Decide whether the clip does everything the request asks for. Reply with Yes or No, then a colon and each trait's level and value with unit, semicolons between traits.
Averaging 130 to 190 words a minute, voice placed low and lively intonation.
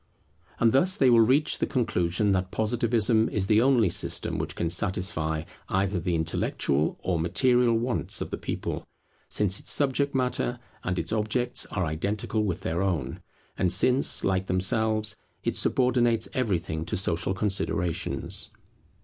No: average, 150 wpm; low, 105 Hz; average, 5.0 semitones